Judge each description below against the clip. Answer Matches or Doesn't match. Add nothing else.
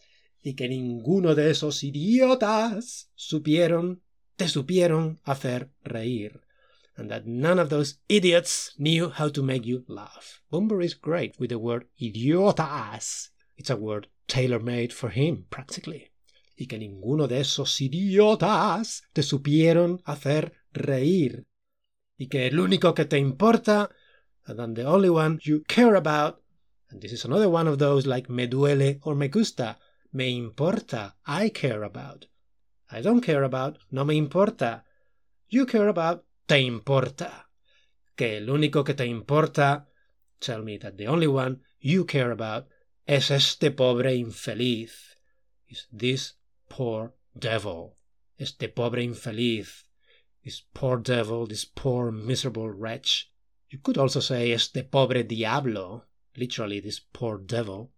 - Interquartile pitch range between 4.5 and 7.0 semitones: Matches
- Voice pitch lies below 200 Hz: Matches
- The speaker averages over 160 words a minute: Doesn't match